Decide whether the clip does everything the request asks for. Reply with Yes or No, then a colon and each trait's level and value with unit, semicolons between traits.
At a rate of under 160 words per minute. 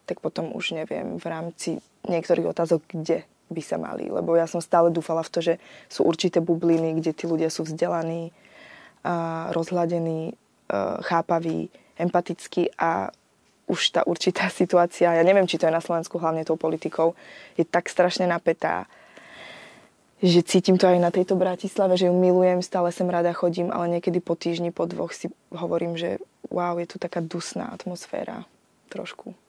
No: fast, 165 wpm